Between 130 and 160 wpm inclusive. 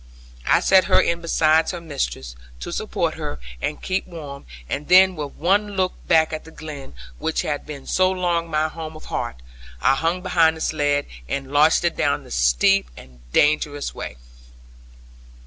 No: average, 175 wpm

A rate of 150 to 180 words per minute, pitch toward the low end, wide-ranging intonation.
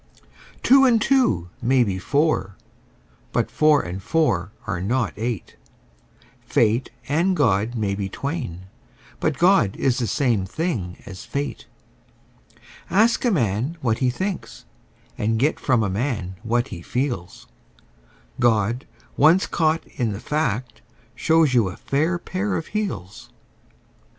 No: slow, 135 wpm; low, 125 Hz; wide, 7.7 semitones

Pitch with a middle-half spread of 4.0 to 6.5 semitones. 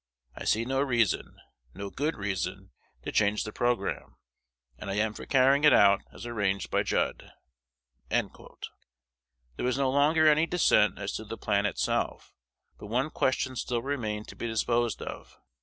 Yes: average, 4.3 semitones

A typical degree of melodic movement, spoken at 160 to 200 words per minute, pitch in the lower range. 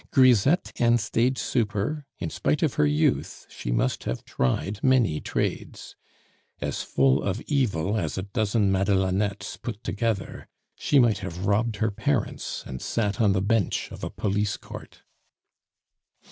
No: average, 3.7 semitones; average, 145 wpm; low, 105 Hz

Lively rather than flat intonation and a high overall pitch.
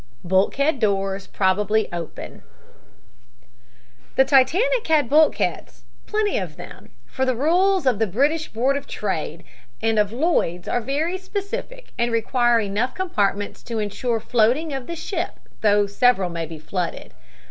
Yes: wide, 7.4 semitones; high, 240 Hz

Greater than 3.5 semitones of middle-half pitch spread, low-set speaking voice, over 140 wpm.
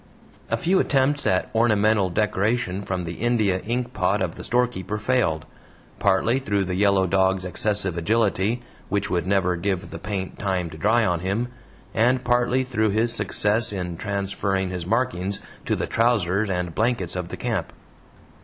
Yes: average, 4.1 semitones; low, 100 Hz; average, 165 wpm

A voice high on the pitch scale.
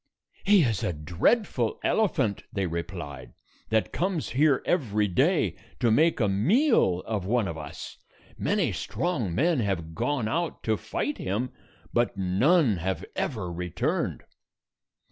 No: low, 110 Hz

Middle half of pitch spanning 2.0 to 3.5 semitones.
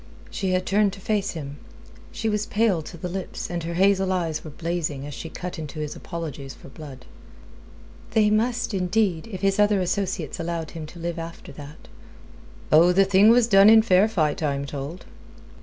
No: average, 4.1 semitones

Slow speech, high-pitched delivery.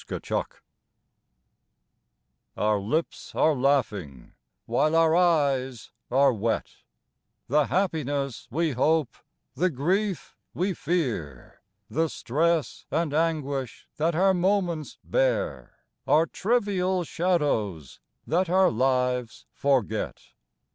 No: slow, 100 wpm; medium, 150 Hz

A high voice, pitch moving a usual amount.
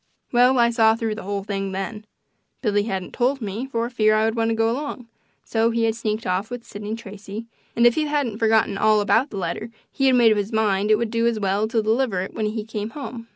No: high, 220 Hz; narrow, 2.1 semitones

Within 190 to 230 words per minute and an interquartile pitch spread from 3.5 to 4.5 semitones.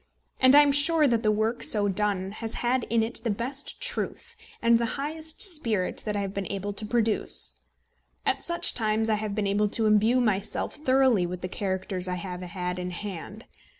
Yes: average, 200 wpm; average, 3.8 semitones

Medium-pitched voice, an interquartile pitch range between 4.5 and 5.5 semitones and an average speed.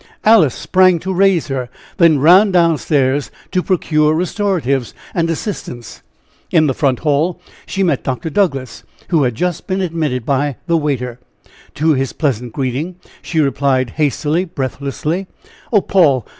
Yes: medium, 155 Hz; average, 4.9 semitones; average, 145 wpm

